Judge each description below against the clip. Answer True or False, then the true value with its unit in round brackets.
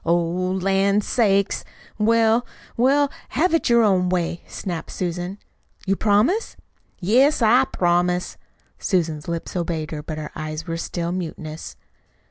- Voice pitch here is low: False (185 Hz)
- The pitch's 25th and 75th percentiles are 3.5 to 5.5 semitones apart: True (4.6 semitones)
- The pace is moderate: False (125 wpm)